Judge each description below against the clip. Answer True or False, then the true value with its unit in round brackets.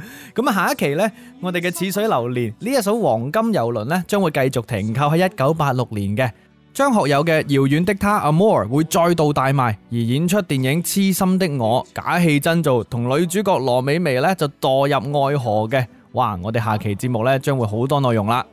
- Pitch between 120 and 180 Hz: True (140 Hz)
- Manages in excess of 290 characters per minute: True (300 characters per minute)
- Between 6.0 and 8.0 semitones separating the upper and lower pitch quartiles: True (6.7 semitones)